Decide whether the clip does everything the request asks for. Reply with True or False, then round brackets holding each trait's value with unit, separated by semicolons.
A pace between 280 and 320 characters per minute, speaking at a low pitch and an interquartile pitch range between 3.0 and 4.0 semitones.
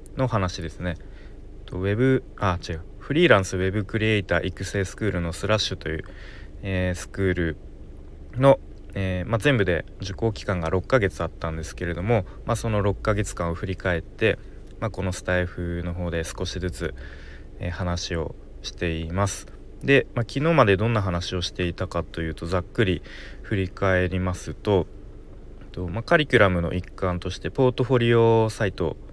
False (335 characters per minute; 95 Hz; 3.3 semitones)